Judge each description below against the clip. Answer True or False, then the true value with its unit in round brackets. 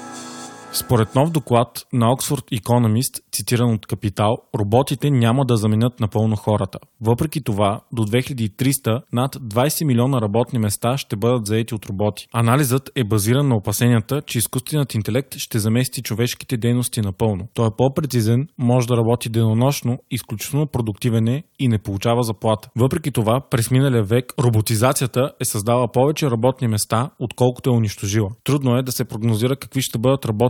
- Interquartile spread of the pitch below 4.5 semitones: True (2.7 semitones)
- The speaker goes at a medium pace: True (155 wpm)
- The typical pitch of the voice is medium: False (120 Hz)